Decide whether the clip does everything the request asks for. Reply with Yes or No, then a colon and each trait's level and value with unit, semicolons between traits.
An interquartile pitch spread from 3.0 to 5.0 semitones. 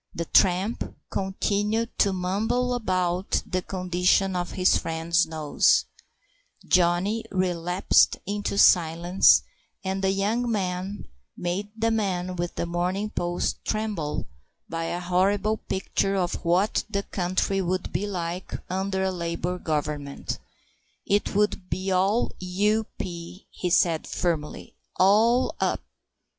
No: narrow, 2.5 semitones